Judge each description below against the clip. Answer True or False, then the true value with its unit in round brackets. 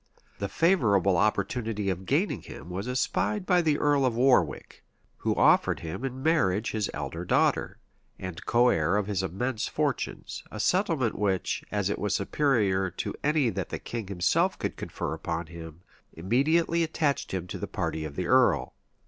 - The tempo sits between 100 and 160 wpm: False (170 wpm)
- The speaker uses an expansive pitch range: True (6.4 semitones)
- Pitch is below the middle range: True (105 Hz)